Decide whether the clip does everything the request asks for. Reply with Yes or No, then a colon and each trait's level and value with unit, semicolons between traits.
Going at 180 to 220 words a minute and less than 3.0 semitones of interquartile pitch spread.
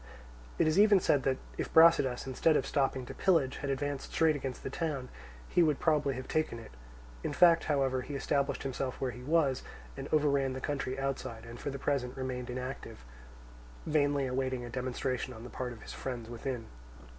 Yes: average, 190 wpm; narrow, 2.4 semitones